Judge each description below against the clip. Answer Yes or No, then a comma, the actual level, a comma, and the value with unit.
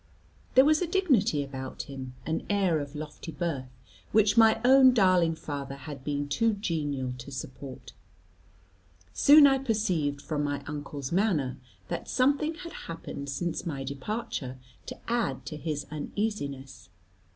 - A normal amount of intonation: No, wide, 7.8 semitones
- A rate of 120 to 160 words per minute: Yes, average, 140 wpm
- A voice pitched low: No, medium, 155 Hz